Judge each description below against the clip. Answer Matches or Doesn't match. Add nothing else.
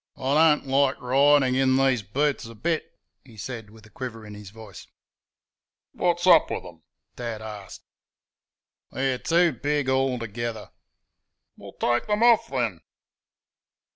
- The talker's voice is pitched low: Matches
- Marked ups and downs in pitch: Doesn't match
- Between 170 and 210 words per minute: Doesn't match